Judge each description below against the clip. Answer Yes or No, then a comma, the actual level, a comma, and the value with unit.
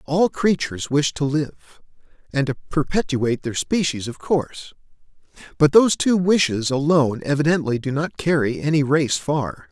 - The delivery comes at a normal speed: Yes, average, 150 wpm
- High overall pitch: No, medium, 145 Hz